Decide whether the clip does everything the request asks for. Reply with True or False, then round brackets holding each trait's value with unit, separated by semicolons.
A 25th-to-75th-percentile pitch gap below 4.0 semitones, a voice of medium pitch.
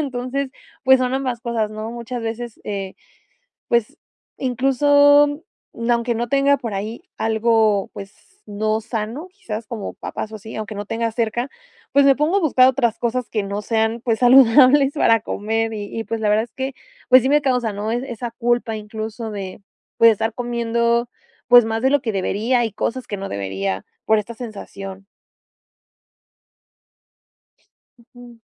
False (2.8 semitones; 230 Hz)